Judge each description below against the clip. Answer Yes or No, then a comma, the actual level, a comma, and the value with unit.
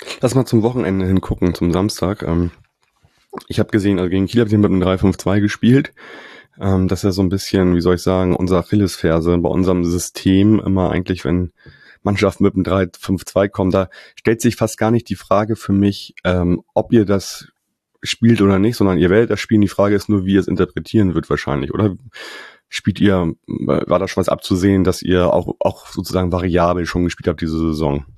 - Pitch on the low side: Yes, very low, 95 Hz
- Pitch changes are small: Yes, narrow, 2.3 semitones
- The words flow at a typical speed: No, fast, 195 wpm